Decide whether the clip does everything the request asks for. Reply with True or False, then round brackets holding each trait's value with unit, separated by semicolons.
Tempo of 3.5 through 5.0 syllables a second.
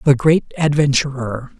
True (4.4 syllables/s)